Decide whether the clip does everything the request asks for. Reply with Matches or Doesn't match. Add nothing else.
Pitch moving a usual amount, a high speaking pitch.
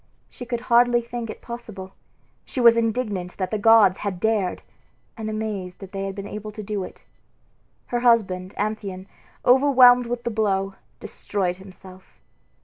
Matches